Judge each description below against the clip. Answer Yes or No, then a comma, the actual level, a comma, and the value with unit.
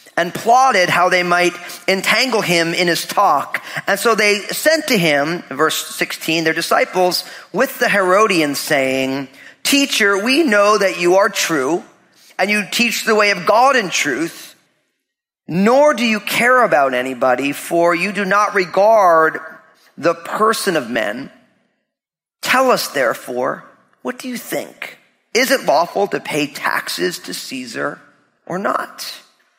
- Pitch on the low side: No, high, 190 Hz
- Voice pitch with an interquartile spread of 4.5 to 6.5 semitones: Yes, average, 5.1 semitones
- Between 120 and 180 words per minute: Yes, average, 145 wpm